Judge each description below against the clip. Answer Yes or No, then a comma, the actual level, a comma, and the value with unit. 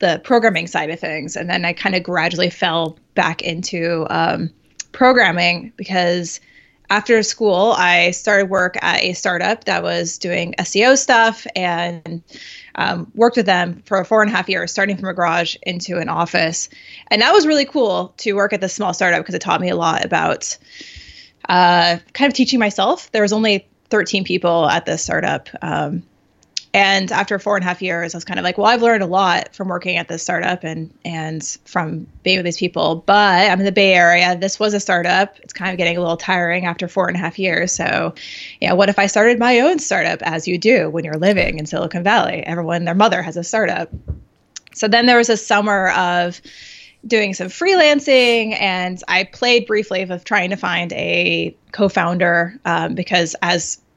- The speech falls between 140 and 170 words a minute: No, average, 200 wpm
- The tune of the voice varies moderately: Yes, average, 3.4 semitones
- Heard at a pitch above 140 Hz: Yes, medium, 185 Hz